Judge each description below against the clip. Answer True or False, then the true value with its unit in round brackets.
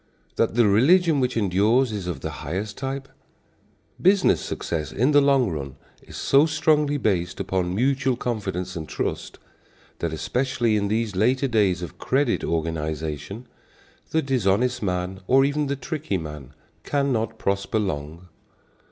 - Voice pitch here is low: True (110 Hz)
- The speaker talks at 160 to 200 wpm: False (145 wpm)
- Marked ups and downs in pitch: True (7.0 semitones)